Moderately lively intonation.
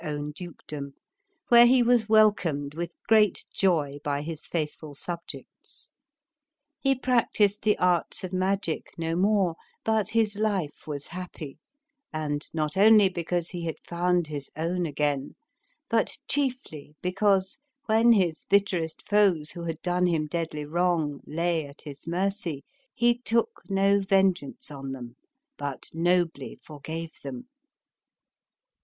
Yes: average, 4.8 semitones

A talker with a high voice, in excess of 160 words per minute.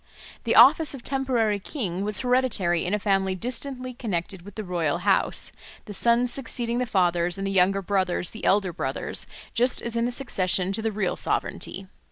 Yes: high, 210 Hz; average, 185 wpm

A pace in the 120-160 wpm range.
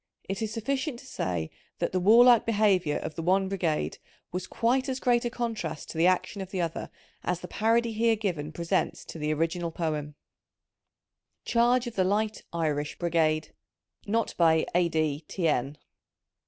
No: average, 170 wpm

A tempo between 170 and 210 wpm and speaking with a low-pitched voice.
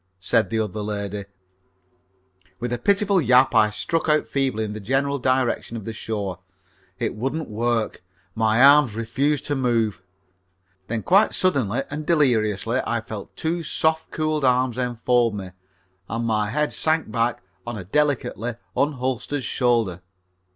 No: average, 145 wpm; low, 120 Hz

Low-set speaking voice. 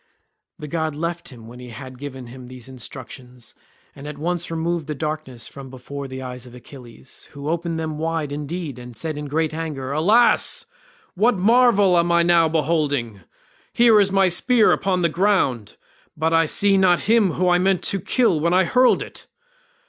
No: medium, 160 Hz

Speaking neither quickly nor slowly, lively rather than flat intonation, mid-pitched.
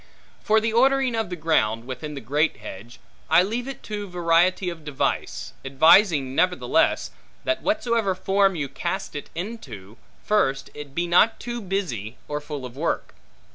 Yes: average, 160 wpm; wide, 7.3 semitones; medium, 175 Hz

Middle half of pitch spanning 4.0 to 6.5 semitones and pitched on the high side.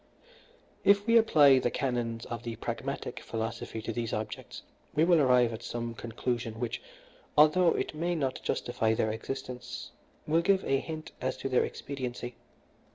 No: average, 4.7 semitones; low, 125 Hz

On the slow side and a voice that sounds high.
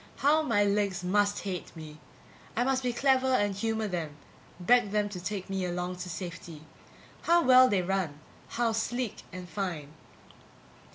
No: average, 160 wpm; high, 200 Hz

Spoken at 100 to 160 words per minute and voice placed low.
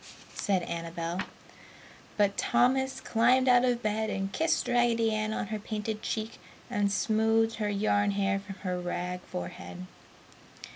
No: average, 140 wpm; high, 210 Hz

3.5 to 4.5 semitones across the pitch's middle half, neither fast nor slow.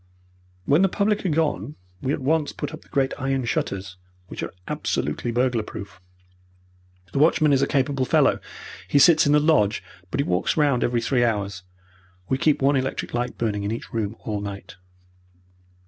No: wide, 5.5 semitones; average, 180 wpm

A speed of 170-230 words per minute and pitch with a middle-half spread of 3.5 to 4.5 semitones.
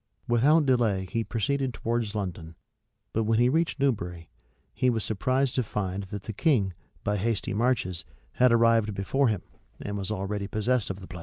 Yes: average, 180 wpm; average, 4.2 semitones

